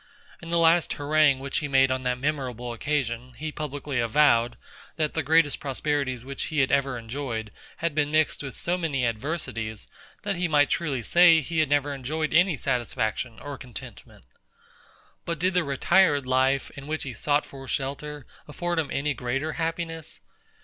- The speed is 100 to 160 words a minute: No, average, 170 wpm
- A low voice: No, medium, 145 Hz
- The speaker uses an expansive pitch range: No, average, 3.4 semitones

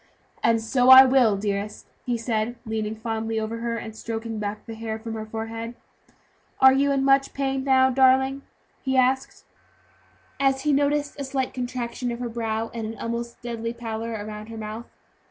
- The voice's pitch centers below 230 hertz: No, high, 235 Hz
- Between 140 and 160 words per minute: No, average, 175 wpm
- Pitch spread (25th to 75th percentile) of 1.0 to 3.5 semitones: Yes, average, 3.0 semitones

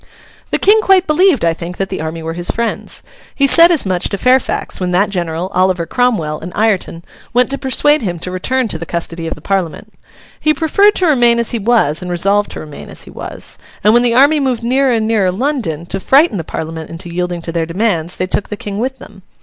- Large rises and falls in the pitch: Yes, wide, 7.0 semitones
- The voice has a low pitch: No, high, 200 Hz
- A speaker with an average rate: No, fast, 230 wpm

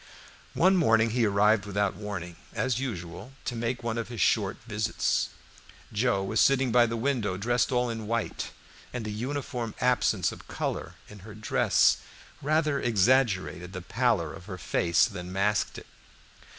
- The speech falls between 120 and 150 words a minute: No, average, 160 wpm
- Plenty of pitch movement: No, average, 3.8 semitones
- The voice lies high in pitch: No, low, 110 Hz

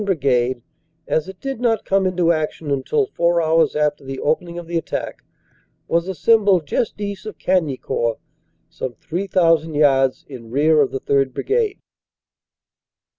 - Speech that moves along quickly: No, average, 145 wpm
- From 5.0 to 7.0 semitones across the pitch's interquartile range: Yes, average, 5.3 semitones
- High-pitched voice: No, medium, 165 Hz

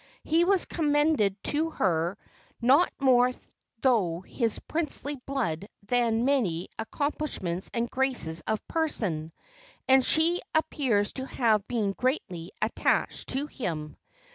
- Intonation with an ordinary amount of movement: No, wide, 6.7 semitones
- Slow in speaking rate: Yes, slow, 120 wpm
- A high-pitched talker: Yes, high, 245 Hz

